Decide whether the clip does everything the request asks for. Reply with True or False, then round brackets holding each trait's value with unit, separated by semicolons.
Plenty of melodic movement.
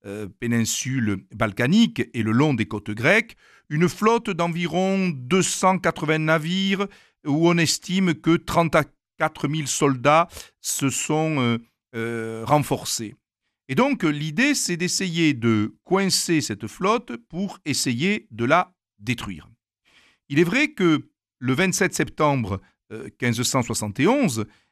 True (7.3 semitones)